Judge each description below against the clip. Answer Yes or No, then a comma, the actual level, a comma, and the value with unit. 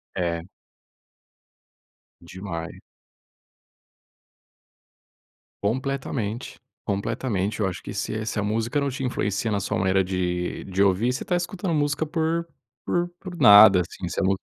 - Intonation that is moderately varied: No, wide, 6.4 semitones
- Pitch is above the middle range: No, low, 110 Hz